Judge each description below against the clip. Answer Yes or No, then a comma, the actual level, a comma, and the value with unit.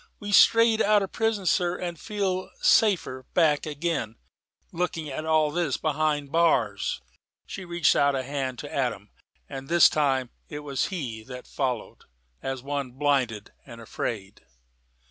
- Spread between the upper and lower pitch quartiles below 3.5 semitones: No, average, 4.8 semitones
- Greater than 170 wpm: No, average, 150 wpm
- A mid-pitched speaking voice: Yes, medium, 150 Hz